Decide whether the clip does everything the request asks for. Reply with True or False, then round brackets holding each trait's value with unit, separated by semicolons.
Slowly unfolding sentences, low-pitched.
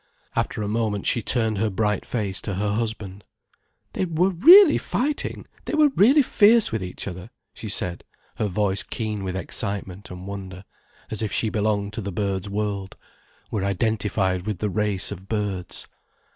False (170 wpm; 105 Hz)